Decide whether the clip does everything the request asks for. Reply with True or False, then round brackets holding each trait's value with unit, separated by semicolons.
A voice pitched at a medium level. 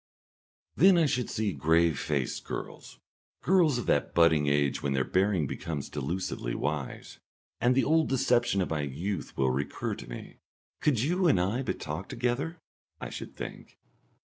False (95 Hz)